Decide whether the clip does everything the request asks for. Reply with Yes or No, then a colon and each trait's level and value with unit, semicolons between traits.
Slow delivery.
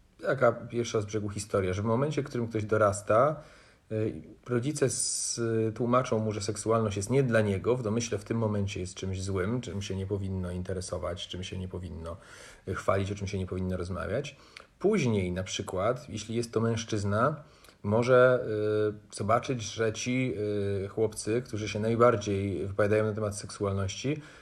No: average, 155 wpm